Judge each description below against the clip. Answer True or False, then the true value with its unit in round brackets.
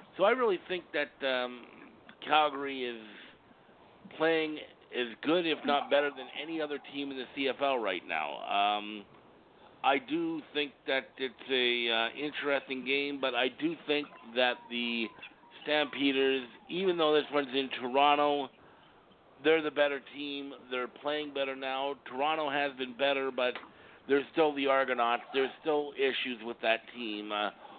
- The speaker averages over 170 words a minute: False (150 wpm)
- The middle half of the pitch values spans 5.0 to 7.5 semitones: False (2.8 semitones)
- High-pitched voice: False (140 Hz)